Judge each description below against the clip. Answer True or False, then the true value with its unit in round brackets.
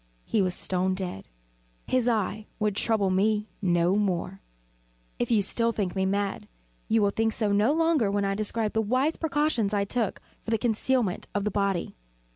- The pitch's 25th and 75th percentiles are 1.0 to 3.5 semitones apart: True (2.7 semitones)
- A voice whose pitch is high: True (210 Hz)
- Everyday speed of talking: True (180 wpm)